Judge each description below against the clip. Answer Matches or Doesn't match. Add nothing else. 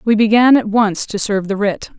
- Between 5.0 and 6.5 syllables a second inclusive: Matches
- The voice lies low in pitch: Doesn't match